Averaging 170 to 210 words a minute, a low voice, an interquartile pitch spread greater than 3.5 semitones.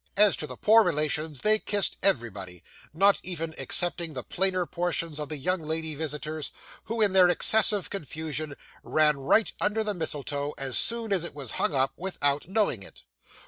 No: average, 175 wpm; medium, 160 Hz; average, 4.8 semitones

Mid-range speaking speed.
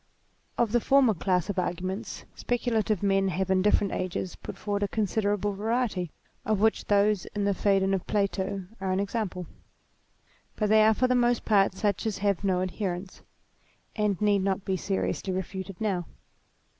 Yes: average, 170 wpm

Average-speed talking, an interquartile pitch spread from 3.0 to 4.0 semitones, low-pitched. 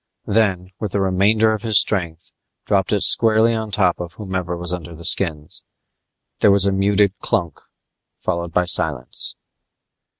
Yes: average, 155 wpm; average, 3.4 semitones; very low, 95 Hz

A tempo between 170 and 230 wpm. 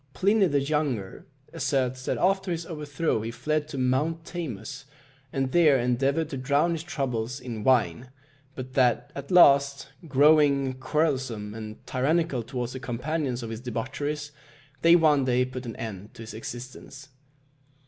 No: average, 150 wpm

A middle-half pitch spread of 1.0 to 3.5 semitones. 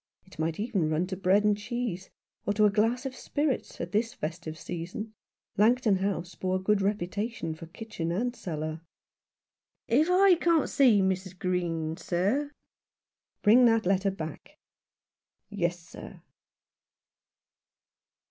No: average, 4.6 semitones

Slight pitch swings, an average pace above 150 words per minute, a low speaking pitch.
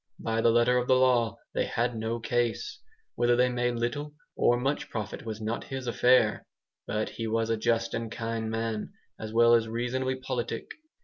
Yes: narrow, 1.6 semitones; average, 185 wpm; low, 115 Hz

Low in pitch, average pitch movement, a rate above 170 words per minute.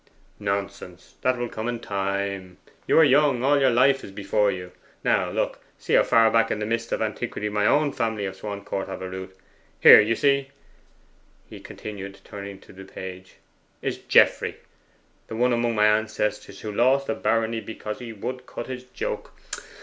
Yes: low, 110 Hz; average, 3.6 semitones; average, 180 wpm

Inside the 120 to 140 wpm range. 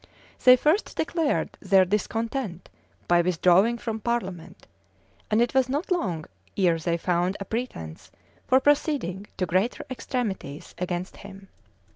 Yes: slow, 135 wpm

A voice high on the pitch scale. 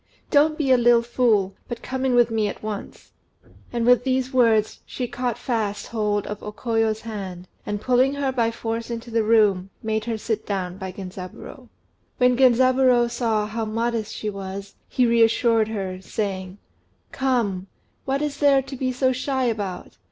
Yes: high, 230 Hz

